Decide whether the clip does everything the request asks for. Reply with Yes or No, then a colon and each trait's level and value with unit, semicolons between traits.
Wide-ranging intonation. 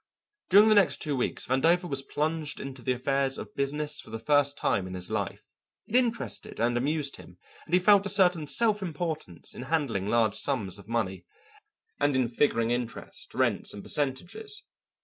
Yes: wide, 6.1 semitones